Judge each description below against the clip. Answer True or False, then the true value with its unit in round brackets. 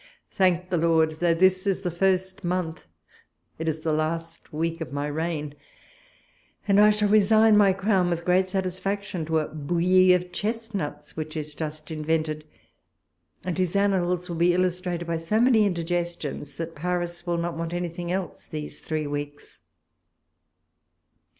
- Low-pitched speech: False (175 Hz)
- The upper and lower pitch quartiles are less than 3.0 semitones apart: True (2.6 semitones)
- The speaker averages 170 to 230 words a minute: False (155 wpm)